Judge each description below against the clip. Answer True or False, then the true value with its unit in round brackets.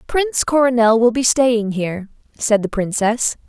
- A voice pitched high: True (235 Hz)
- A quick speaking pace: False (155 wpm)